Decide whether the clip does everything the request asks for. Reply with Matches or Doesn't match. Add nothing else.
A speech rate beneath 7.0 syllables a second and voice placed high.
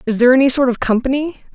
Doesn't match